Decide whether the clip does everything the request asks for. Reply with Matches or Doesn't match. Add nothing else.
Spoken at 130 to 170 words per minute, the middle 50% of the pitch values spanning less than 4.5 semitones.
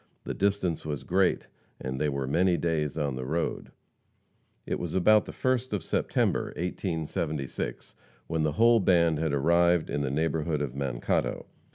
Matches